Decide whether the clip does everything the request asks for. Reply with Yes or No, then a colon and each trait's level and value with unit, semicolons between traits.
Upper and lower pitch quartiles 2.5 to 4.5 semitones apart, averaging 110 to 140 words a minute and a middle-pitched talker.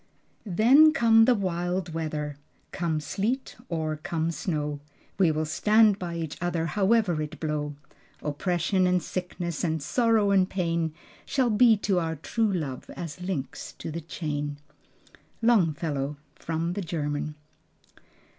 Yes: average, 4.2 semitones; slow, 135 wpm; medium, 170 Hz